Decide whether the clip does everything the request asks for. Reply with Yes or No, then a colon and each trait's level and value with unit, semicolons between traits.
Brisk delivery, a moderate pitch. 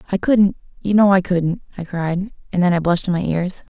Yes: fast, 210 wpm; medium, 180 Hz